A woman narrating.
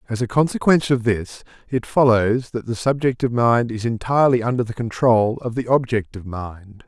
No: male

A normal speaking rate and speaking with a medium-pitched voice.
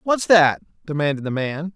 Yes: average, 170 wpm; medium, 160 Hz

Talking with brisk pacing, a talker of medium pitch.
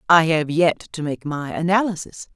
No: average, 180 wpm; medium, 165 Hz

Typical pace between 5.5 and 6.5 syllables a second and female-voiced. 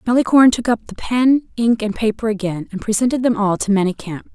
Yes: 6.0 syllables/s; female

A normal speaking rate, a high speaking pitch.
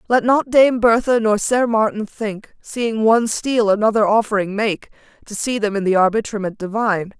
Yes: average, 175 wpm; high, 220 Hz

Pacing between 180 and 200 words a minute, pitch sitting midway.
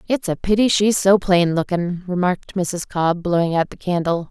Yes: average, 195 wpm; medium, 180 Hz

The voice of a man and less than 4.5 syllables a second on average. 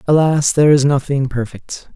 No: male; 5.1 syllables/s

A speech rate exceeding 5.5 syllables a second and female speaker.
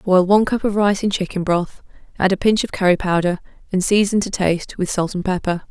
Yes: 5.8 syllables/s; female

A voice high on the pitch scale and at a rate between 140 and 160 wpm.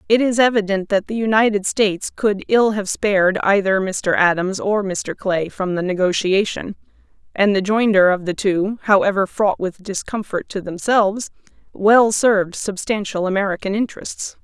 Yes: high, 200 Hz; average, 155 wpm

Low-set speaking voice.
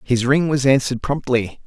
Yes: low, 130 Hz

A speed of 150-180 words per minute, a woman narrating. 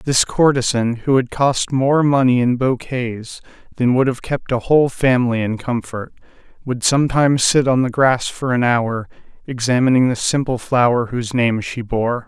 No: average, 170 wpm; male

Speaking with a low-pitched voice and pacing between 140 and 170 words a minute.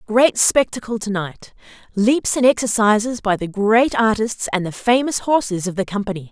No: high, 220 Hz; average, 160 wpm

